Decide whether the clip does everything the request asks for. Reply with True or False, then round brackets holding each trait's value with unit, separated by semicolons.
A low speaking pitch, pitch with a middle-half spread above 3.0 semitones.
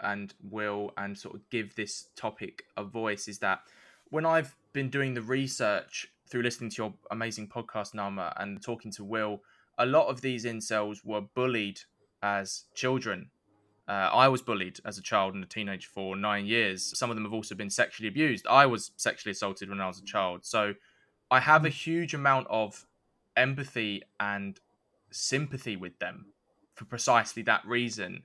True (110 Hz; 3.8 semitones)